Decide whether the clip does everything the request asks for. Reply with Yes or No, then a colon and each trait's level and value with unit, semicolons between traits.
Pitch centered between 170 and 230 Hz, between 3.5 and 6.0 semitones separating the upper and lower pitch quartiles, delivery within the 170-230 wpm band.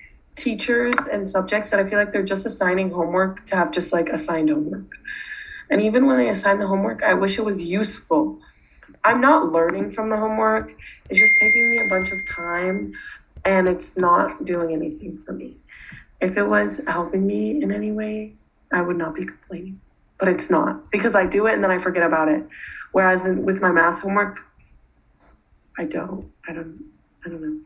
Yes: high, 190 Hz; average, 4.1 semitones; average, 190 wpm